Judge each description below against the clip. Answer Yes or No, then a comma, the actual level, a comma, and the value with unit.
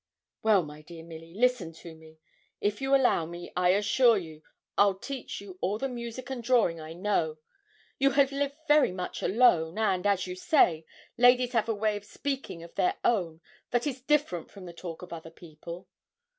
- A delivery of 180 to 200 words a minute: Yes, average, 190 wpm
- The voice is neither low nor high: No, high, 200 Hz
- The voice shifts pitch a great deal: Yes, wide, 6.8 semitones